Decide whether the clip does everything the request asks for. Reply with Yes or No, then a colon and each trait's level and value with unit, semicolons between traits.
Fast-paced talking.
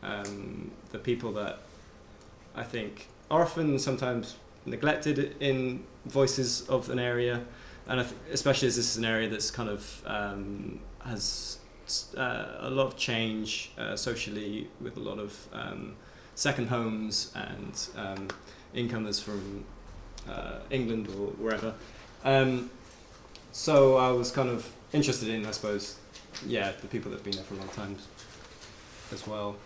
No: average, 150 wpm